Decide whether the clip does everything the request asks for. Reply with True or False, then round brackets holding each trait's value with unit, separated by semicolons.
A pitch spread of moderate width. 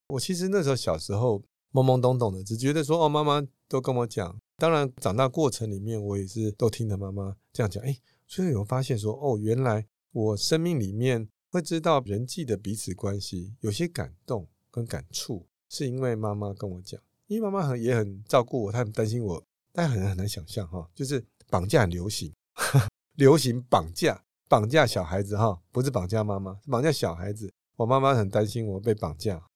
True (5.0 semitones)